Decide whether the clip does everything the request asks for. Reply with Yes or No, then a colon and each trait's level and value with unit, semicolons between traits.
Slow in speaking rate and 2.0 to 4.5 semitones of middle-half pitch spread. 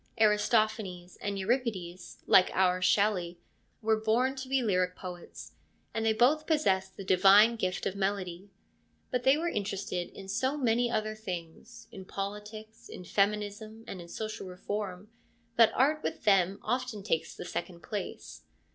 No: average, 150 wpm; average, 3.3 semitones